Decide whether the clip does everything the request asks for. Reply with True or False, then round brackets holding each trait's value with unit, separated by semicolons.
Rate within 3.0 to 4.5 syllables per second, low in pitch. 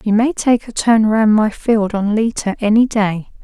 False (4.4 syllables/s; 215 Hz)